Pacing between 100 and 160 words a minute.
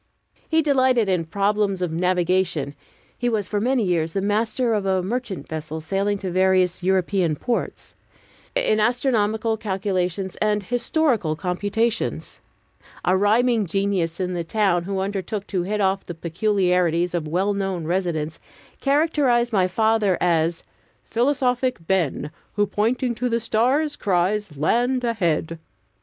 Yes: slow, 135 wpm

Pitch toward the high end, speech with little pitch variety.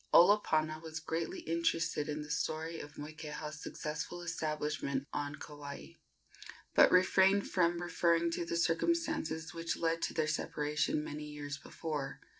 No: medium, 160 Hz; narrow, 2.0 semitones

